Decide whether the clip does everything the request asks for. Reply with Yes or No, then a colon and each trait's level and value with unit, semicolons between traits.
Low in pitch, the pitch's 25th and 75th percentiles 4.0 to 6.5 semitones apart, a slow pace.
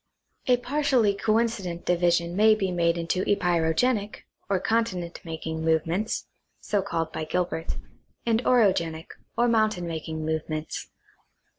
No: medium, 180 Hz; average, 4.9 semitones; slow, 120 wpm